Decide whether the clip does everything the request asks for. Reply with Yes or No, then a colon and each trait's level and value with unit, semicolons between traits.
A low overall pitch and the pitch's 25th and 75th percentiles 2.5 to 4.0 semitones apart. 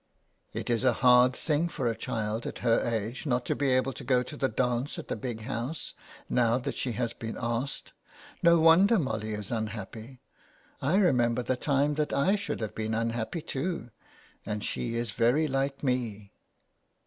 Yes: low, 125 Hz; average, 3.3 semitones